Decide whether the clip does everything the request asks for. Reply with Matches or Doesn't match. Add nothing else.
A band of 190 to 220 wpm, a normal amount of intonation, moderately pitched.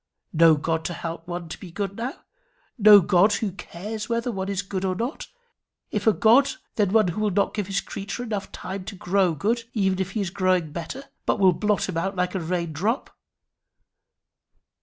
Doesn't match